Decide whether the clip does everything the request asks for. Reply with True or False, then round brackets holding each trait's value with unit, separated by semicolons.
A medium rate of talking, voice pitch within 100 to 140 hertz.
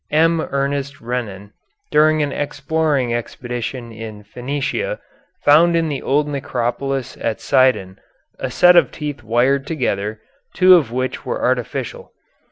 False (130 wpm; 135 Hz)